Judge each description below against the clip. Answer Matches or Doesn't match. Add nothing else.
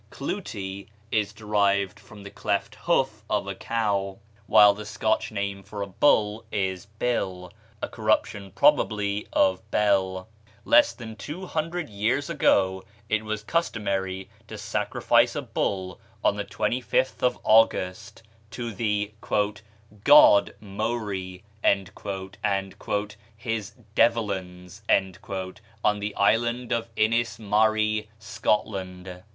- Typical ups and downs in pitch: Doesn't match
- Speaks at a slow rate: Matches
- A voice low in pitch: Matches